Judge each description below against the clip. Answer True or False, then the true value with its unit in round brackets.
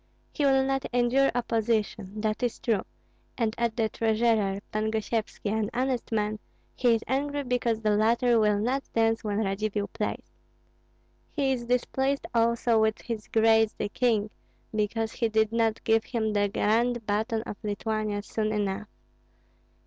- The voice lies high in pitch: True (225 Hz)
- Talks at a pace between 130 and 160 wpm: True (155 wpm)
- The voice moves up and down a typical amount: False (2.0 semitones)